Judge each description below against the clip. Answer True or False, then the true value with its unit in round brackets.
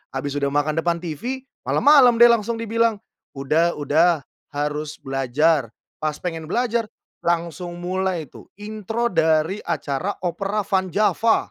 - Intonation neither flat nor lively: False (5.8 semitones)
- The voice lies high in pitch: False (175 Hz)